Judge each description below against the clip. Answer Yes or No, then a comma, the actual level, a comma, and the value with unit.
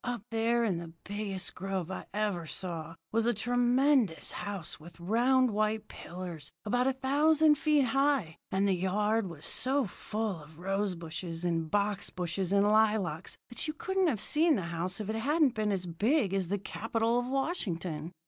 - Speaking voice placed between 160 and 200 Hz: No, high, 210 Hz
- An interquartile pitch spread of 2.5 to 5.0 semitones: No, wide, 5.6 semitones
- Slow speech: No, average, 175 wpm